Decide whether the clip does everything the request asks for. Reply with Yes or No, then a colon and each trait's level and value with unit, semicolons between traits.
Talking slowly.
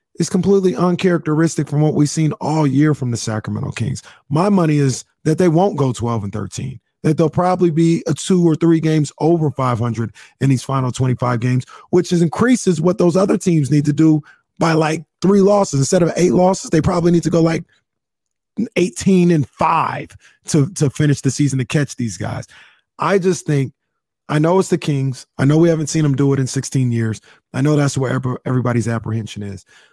No: fast, 205 wpm